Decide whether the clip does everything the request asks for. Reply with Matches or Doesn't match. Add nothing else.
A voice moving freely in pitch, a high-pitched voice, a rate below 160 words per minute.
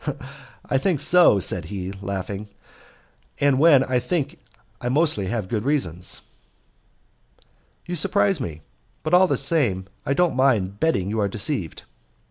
Doesn't match